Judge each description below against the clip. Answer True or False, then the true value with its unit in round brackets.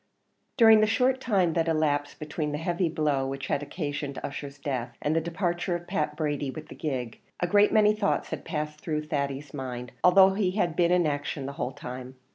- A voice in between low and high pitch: True (155 Hz)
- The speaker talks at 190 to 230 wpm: True (205 wpm)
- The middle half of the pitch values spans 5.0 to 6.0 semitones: False (4.1 semitones)